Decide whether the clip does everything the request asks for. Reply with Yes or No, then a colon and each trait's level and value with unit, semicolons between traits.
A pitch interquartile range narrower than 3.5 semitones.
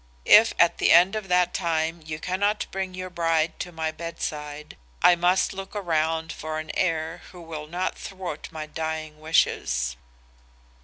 Yes: narrow, 2.4 semitones